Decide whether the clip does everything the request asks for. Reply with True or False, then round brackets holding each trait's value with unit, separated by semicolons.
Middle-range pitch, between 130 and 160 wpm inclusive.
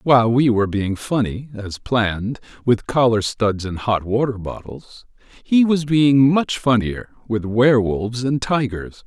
False (115 Hz; 150 wpm)